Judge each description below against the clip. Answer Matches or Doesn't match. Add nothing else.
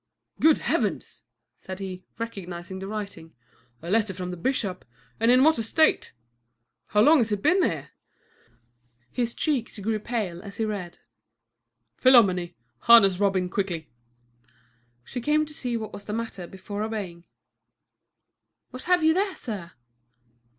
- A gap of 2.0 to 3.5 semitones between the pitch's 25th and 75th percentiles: Doesn't match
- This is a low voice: Doesn't match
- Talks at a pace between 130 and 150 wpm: Matches